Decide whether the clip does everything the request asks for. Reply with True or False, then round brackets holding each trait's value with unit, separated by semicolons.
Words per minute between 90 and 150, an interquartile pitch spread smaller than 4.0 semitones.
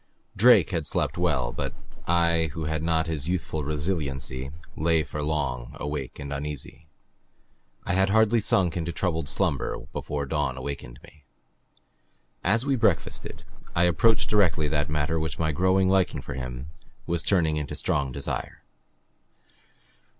True (145 wpm; 3.6 semitones)